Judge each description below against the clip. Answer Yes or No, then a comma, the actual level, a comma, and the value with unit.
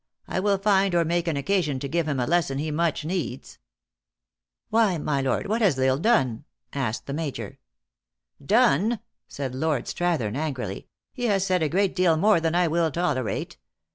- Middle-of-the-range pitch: Yes, medium, 160 Hz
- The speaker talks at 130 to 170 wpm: No, average, 200 wpm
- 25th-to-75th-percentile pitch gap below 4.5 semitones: No, wide, 5.4 semitones